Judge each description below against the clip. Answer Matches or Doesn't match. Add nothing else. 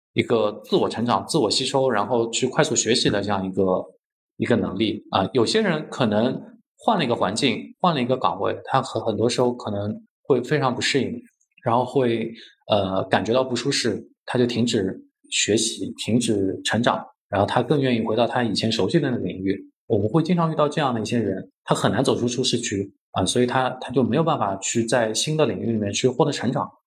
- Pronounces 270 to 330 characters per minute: Matches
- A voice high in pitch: Doesn't match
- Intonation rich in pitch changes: Doesn't match